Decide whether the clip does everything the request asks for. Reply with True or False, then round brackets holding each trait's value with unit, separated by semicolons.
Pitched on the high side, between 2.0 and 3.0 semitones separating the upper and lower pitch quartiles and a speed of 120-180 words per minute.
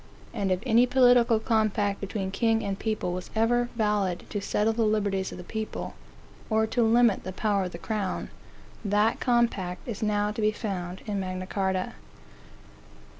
True (210 Hz; 2.7 semitones; 170 wpm)